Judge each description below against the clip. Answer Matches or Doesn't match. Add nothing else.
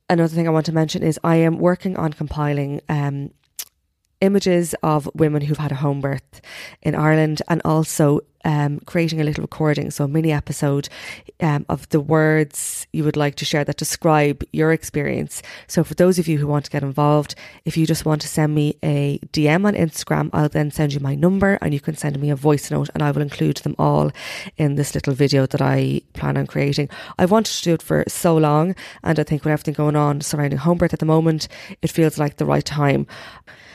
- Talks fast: Matches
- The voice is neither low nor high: Matches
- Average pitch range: Doesn't match